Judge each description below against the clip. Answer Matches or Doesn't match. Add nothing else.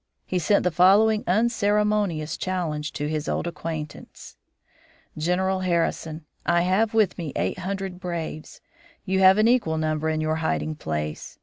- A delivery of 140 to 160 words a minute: Matches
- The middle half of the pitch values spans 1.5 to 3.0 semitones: Doesn't match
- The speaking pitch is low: Doesn't match